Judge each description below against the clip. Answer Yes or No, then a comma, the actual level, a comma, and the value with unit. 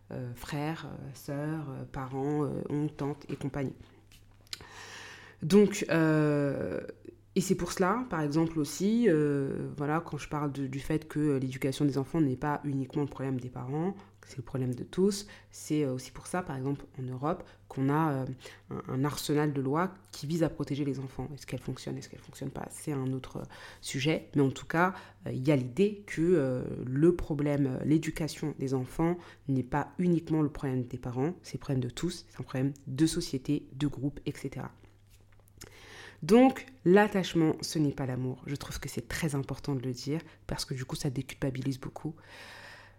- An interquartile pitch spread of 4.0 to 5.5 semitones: No, average, 3.2 semitones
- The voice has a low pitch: No, medium, 145 Hz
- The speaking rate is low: No, average, 185 wpm